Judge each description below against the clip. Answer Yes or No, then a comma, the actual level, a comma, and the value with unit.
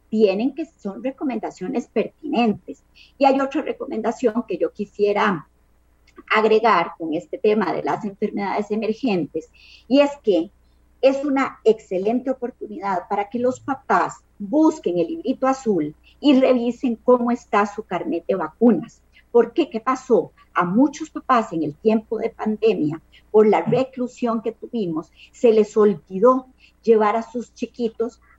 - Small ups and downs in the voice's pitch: No, average, 3.8 semitones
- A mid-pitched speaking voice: No, high, 230 Hz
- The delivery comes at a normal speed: Yes, average, 140 wpm